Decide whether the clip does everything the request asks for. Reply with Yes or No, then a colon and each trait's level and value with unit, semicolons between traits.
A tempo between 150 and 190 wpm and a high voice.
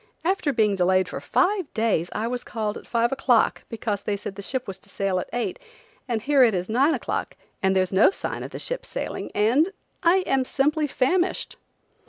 No: average, 200 wpm; high, 235 Hz